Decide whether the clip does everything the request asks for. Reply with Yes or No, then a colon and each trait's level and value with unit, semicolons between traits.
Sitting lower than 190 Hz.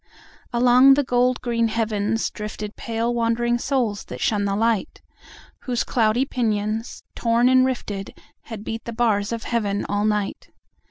No: high, 230 Hz